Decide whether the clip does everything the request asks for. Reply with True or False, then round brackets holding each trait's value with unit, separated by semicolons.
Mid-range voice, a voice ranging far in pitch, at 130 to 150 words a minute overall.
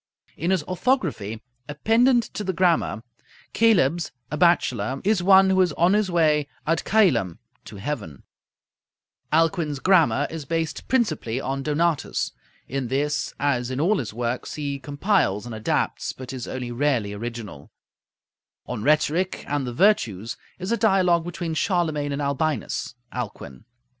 True (150 Hz; 6.3 semitones; 145 wpm)